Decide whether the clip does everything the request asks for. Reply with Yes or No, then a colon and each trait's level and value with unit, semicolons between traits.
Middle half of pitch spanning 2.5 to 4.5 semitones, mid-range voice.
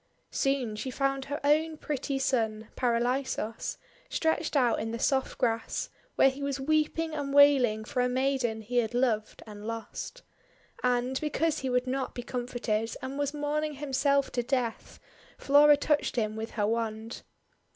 No: average, 3.5 semitones; very high, 260 Hz